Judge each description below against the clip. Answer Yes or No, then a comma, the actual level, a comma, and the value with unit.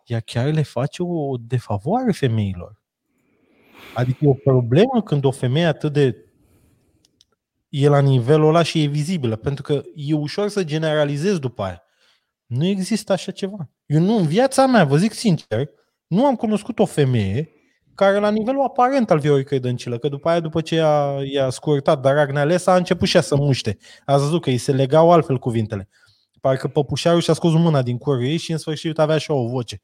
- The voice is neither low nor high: Yes, medium, 150 Hz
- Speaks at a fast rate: Yes, fast, 185 wpm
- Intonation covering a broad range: No, average, 4.6 semitones